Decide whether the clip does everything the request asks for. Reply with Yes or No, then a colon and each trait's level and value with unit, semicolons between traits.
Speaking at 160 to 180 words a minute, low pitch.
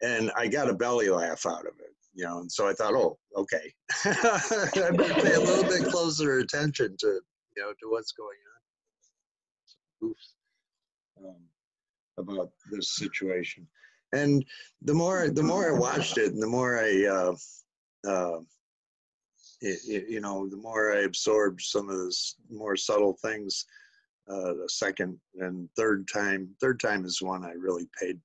Yes: average, 170 wpm; low, 110 Hz